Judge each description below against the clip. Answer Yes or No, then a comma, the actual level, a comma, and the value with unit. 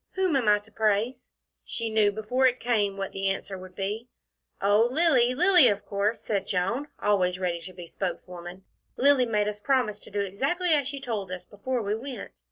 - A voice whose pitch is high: Yes, high, 210 Hz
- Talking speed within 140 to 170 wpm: No, average, 195 wpm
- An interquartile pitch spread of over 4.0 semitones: Yes, average, 4.4 semitones